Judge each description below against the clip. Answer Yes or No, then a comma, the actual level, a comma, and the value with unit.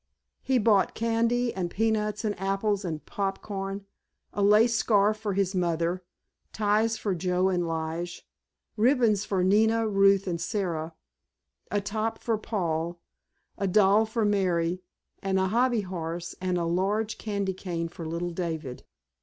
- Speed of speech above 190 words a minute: No, average, 145 wpm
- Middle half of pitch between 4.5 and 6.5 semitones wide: No, average, 3.4 semitones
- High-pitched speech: Yes, high, 195 Hz